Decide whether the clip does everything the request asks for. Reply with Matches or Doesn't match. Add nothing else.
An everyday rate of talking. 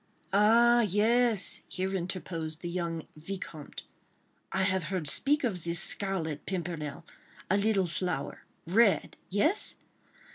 Doesn't match